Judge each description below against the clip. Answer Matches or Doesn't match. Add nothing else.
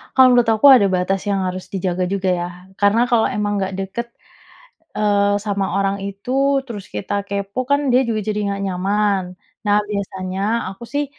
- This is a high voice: Matches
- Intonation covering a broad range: Doesn't match